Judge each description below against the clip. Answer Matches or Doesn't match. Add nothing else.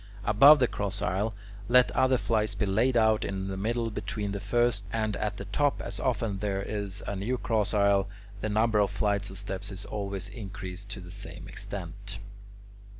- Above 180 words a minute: Matches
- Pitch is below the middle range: Matches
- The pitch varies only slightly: Matches